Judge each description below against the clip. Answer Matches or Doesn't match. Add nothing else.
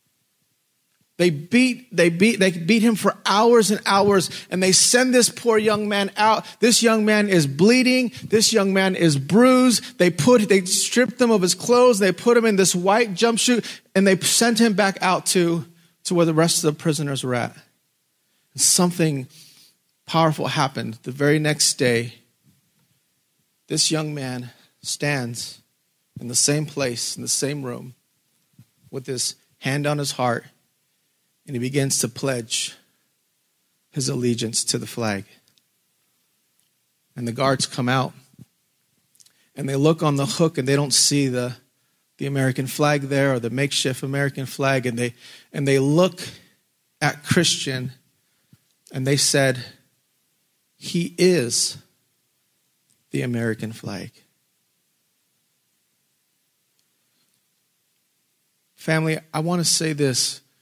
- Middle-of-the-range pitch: Matches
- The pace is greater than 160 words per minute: Doesn't match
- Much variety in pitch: Matches